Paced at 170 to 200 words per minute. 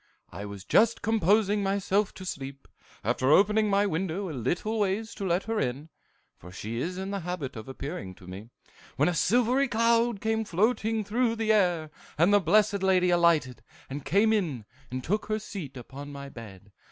Yes: average, 180 wpm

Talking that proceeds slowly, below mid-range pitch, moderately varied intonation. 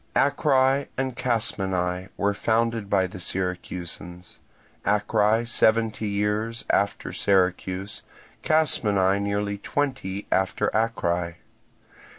Yes: slow, 90 wpm; low, 100 Hz; average, 3.4 semitones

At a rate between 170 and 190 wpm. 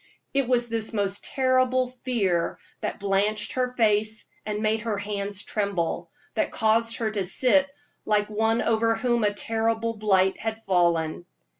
No: average, 150 wpm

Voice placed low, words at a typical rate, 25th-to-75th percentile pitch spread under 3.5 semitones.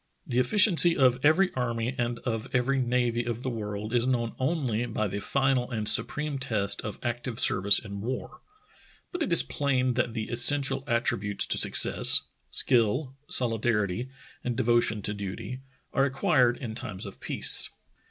Yes: low, 120 Hz; average, 165 wpm; average, 3.0 semitones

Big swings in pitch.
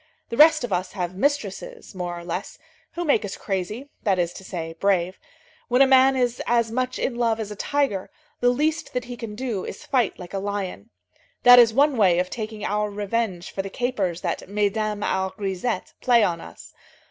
No: average, 4.5 semitones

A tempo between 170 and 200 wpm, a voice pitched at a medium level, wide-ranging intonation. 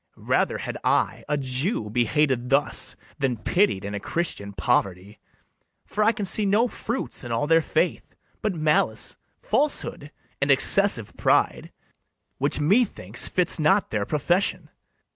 No: average, 145 wpm; medium, 150 Hz; wide, 8.6 semitones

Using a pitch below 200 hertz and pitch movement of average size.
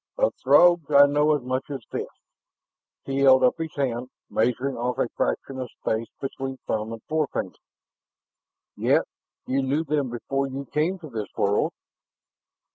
Yes: low, 135 Hz; average, 3.0 semitones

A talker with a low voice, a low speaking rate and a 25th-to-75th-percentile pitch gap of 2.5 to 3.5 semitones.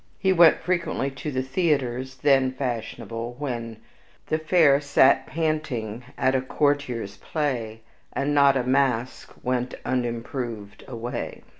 Yes: low, 130 Hz; slow, 125 wpm; average, 3.2 semitones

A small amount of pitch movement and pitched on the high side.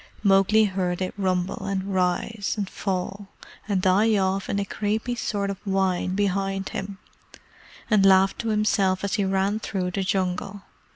Yes: narrow, 1.3 semitones; high, 195 Hz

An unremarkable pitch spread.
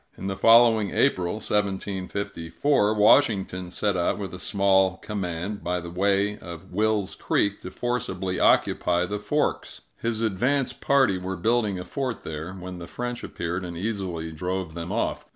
Yes: average, 3.2 semitones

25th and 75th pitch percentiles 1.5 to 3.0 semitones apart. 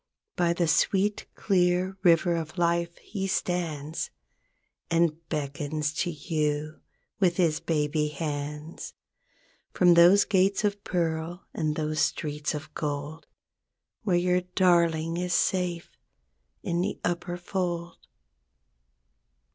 Yes: narrow, 2.6 semitones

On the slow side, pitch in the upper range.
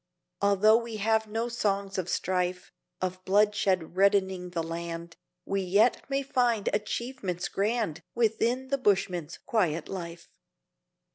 Yes: slow, 125 wpm; high, 200 Hz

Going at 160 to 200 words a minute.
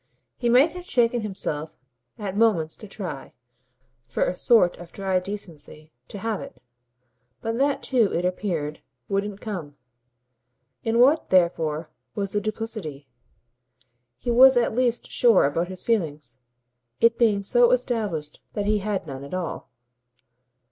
No: average, 140 wpm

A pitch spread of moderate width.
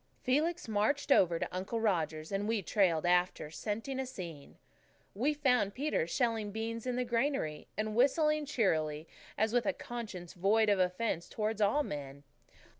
No: wide, 5.8 semitones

